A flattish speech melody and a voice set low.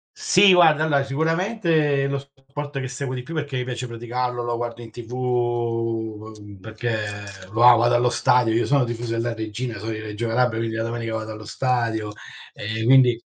No: average, 3.0 semitones; low, 120 Hz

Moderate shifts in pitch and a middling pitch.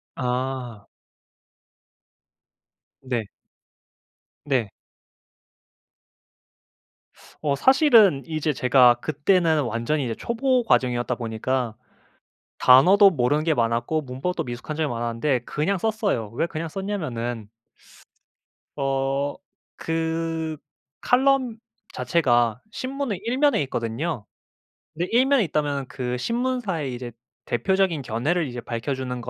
No: wide, 6.7 semitones; medium, 145 Hz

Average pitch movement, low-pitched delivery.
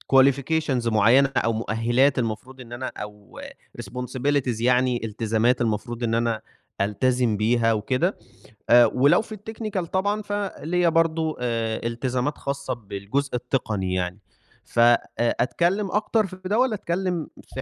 No: wide, 6.2 semitones; low, 125 Hz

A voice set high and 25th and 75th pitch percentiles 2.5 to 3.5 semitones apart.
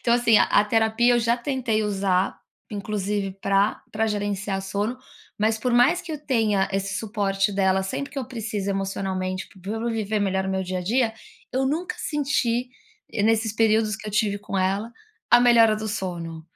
Yes: high, 210 Hz; average, 3.0 semitones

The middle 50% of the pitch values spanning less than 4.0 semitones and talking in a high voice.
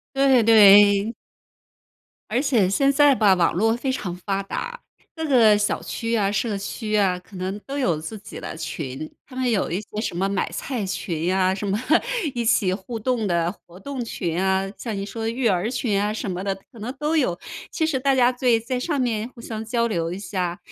No: average, 4.5 semitones; high, 210 Hz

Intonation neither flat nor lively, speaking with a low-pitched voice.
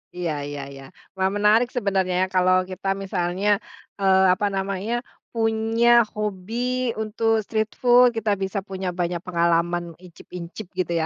No: average, 3.3 semitones; high, 190 Hz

